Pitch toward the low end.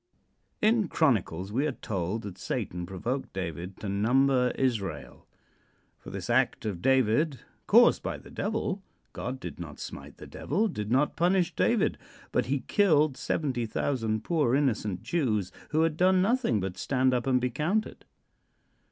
Yes: low, 130 Hz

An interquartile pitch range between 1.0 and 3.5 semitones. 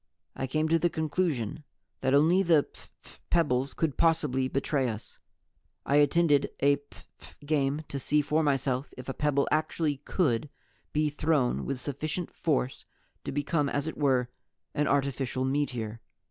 Yes: average, 2.7 semitones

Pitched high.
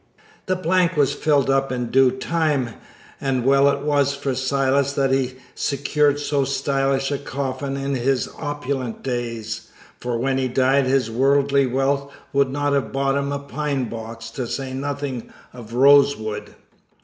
No: low, 135 Hz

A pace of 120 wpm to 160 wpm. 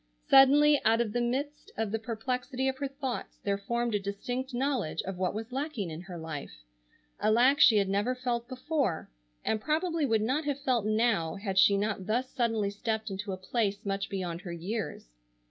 No: average, 195 wpm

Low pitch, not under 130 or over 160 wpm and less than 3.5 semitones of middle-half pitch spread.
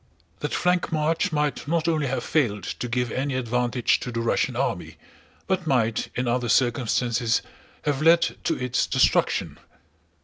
No: low, 130 Hz; average, 150 wpm; average, 4.4 semitones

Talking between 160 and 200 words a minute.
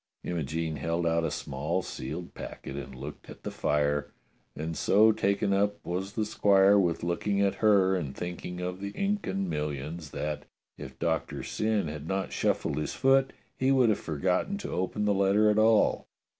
Yes: average, 175 wpm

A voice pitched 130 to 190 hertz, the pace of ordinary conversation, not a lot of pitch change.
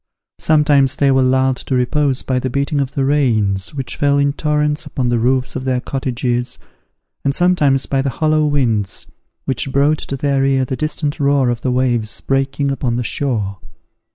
Yes: low, 135 Hz; average, 180 wpm; narrow, 2.3 semitones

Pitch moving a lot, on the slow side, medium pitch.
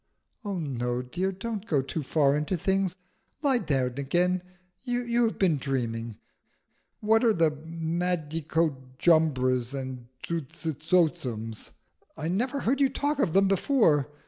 Yes: wide, 6.2 semitones; slow, 125 wpm; medium, 160 Hz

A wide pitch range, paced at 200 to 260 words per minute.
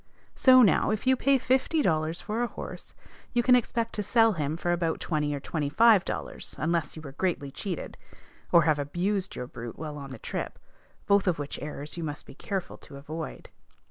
Yes: wide, 6.5 semitones; fast, 205 wpm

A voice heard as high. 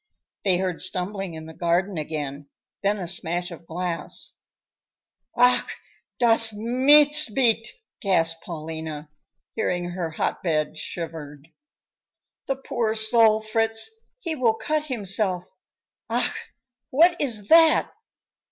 Yes: high, 195 Hz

